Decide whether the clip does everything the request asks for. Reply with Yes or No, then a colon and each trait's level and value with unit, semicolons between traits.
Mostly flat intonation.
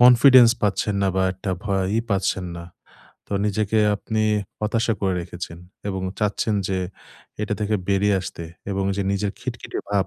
Yes: narrow, 2.0 semitones